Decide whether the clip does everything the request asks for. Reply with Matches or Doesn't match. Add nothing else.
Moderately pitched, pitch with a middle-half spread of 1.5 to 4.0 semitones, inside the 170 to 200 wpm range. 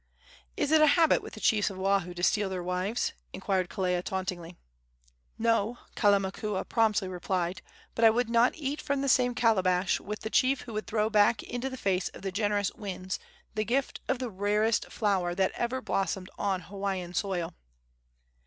Doesn't match